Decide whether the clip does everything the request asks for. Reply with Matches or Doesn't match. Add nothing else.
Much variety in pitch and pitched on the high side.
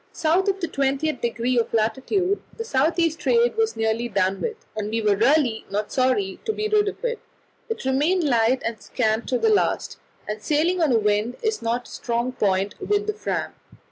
Matches